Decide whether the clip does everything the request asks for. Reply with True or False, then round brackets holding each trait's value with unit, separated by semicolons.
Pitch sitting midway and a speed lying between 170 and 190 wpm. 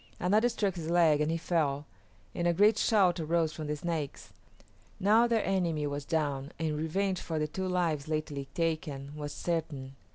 True (160 Hz; 175 wpm)